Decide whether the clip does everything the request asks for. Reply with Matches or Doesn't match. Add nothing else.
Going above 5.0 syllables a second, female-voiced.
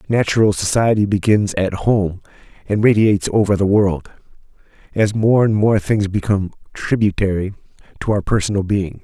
Doesn't match